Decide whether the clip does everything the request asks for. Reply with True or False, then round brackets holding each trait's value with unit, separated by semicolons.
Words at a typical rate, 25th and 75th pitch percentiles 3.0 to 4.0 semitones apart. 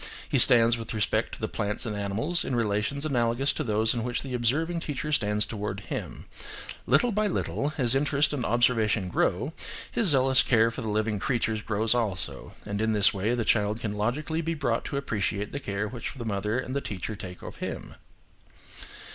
False (195 wpm; 4.4 semitones)